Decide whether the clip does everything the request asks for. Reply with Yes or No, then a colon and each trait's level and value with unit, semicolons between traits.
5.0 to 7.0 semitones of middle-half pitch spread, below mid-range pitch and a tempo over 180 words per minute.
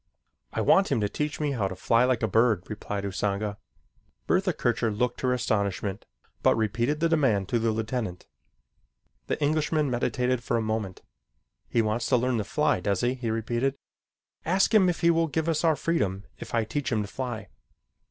Yes: average, 5.3 semitones; low, 120 Hz; average, 190 wpm